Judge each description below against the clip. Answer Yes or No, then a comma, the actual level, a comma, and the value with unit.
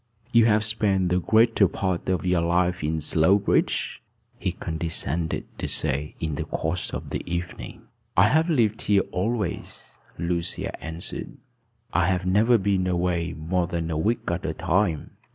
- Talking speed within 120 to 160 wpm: Yes, average, 155 wpm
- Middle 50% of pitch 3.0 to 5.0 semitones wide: Yes, average, 3.4 semitones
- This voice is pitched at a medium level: No, very low, 90 Hz